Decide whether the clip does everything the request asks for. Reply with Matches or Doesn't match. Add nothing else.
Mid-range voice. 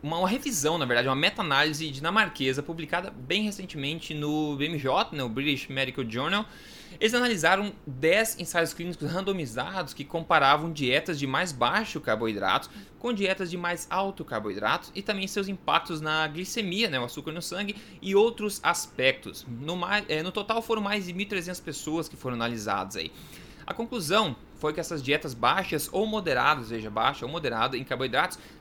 Matches